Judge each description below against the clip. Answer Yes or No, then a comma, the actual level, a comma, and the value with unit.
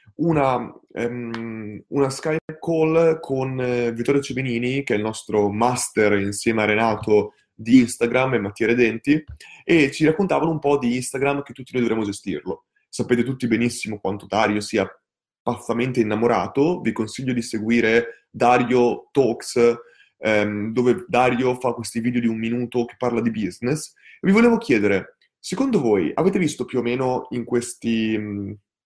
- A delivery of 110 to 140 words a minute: No, average, 155 wpm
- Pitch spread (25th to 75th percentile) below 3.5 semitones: Yes, average, 2.8 semitones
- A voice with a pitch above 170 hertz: No, low, 120 Hz